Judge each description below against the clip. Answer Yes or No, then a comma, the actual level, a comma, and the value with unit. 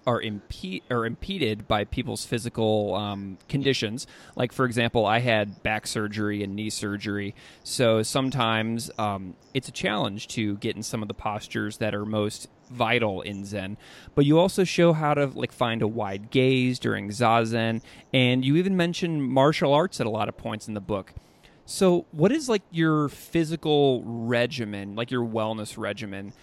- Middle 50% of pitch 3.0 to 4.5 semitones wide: Yes, average, 3.8 semitones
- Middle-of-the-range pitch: No, low, 115 Hz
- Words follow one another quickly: No, average, 175 wpm